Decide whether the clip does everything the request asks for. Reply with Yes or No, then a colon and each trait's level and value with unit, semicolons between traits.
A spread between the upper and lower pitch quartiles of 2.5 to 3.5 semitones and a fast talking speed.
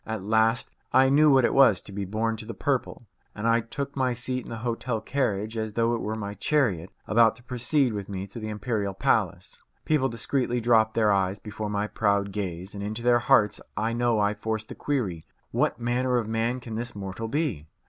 Yes: average, 2.8 semitones; fast, 215 wpm